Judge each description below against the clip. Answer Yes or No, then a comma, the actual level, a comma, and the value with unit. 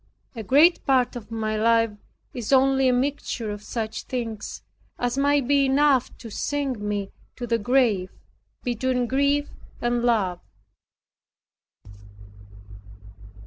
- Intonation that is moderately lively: Yes, average, 3.4 semitones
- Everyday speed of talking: No, slow, 120 wpm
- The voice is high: Yes, high, 245 Hz